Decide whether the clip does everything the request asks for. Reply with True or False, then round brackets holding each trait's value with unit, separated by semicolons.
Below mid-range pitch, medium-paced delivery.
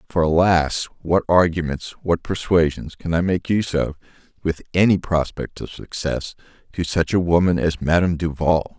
True (85 Hz; 155 wpm)